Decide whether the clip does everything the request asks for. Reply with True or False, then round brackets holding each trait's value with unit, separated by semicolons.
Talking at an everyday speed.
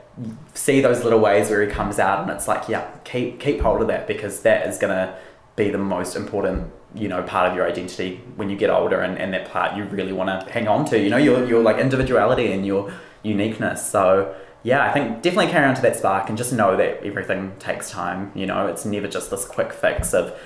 False (240 wpm)